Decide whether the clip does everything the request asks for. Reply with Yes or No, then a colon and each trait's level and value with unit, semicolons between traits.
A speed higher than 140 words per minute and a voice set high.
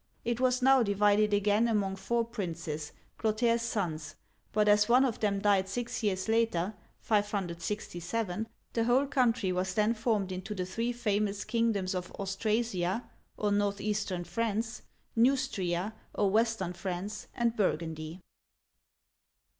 No: slow, 135 wpm; high, 210 Hz